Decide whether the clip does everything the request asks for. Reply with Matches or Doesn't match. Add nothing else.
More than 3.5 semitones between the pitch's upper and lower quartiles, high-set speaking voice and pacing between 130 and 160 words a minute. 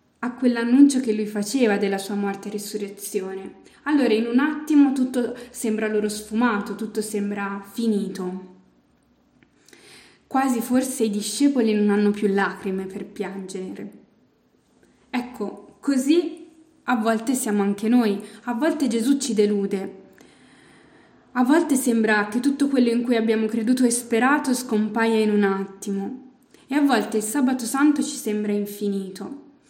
Matches